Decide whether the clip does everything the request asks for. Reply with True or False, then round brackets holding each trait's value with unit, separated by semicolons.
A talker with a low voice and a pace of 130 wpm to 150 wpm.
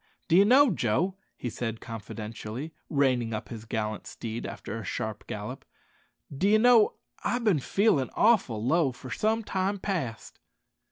True (130 Hz; 145 wpm)